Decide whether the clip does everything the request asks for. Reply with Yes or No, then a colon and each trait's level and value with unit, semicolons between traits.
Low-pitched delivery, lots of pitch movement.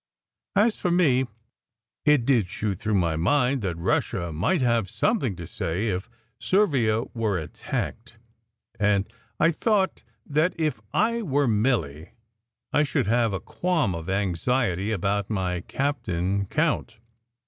Yes: low, 110 Hz; wide, 7.3 semitones